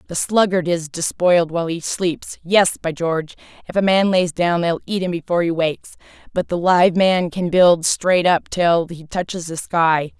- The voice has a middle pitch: Yes, medium, 175 Hz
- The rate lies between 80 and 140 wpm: No, average, 190 wpm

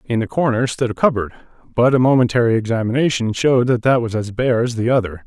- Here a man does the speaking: Yes, male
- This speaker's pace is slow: No, fast, 205 wpm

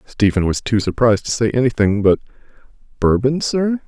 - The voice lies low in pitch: Yes, low, 120 Hz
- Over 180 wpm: No, average, 155 wpm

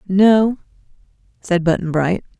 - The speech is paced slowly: Yes, slow, 100 wpm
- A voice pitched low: No, medium, 185 Hz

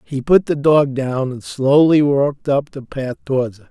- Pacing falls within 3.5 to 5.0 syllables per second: Yes, 4.6 syllables/s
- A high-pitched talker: No, medium, 140 Hz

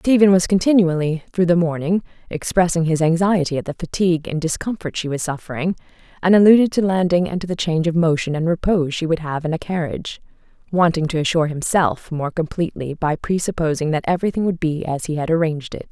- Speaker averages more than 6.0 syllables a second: Yes, 6.3 syllables/s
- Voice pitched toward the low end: No, medium, 170 Hz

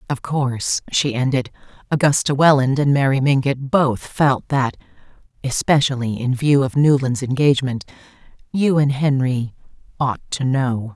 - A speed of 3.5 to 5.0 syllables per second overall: Yes, 4.6 syllables/s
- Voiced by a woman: Yes, female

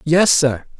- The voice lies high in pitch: No, medium, 150 Hz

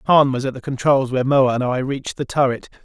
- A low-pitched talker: Yes, low, 130 Hz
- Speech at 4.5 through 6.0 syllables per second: Yes, 5.9 syllables/s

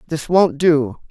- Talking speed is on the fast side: No, average, 165 wpm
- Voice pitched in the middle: Yes, medium, 155 Hz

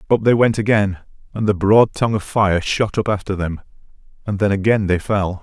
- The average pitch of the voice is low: Yes, low, 100 Hz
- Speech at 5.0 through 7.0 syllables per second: Yes, 5.4 syllables/s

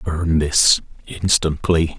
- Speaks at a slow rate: Yes, slow, 90 wpm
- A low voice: Yes, very low, 80 Hz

